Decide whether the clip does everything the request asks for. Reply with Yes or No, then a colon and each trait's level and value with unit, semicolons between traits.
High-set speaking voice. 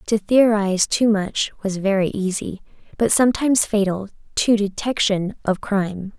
Yes: high, 205 Hz